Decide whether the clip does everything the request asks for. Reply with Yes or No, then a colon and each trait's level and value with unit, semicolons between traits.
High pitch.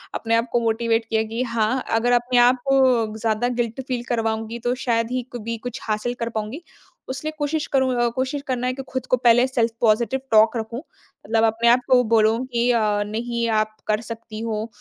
Yes: high, 235 Hz